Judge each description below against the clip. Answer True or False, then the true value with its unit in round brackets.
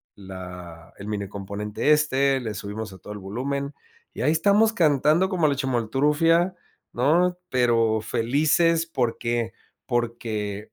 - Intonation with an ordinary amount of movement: False (6.4 semitones)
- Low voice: True (125 Hz)